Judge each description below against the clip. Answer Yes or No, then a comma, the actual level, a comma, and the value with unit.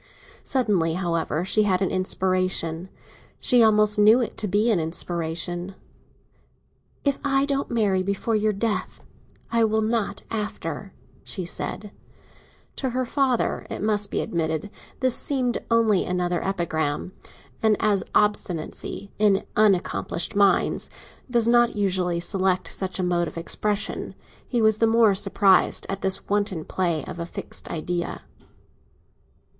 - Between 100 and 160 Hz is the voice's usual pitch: No, high, 200 Hz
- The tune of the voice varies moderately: Yes, average, 3.6 semitones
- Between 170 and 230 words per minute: No, slow, 135 wpm